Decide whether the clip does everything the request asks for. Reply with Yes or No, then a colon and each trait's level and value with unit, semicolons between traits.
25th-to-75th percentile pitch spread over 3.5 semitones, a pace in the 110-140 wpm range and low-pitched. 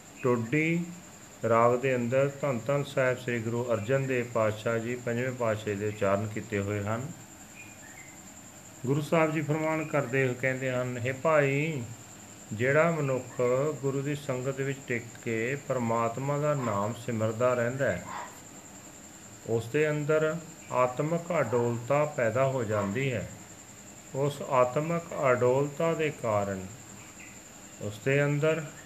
Yes: average, 4.6 semitones; average, 125 wpm; low, 125 Hz